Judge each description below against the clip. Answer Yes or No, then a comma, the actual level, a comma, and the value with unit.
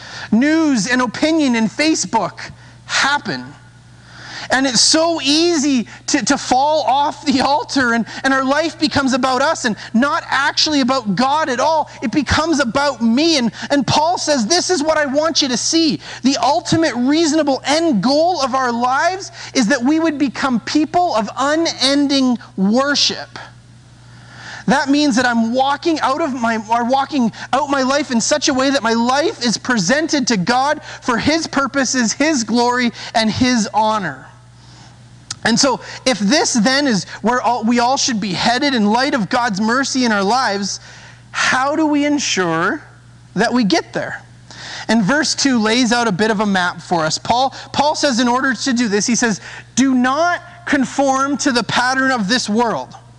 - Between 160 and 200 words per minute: Yes, average, 175 wpm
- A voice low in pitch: No, very high, 260 Hz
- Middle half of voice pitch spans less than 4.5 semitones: Yes, average, 4.0 semitones